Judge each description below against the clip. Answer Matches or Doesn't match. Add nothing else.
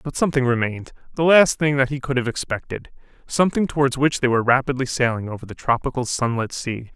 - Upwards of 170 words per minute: Matches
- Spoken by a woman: Doesn't match